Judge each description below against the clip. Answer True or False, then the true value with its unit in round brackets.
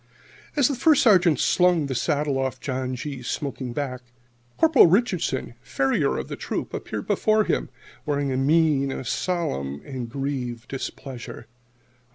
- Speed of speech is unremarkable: True (145 wpm)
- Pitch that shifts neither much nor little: True (4.8 semitones)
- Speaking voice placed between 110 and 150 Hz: True (140 Hz)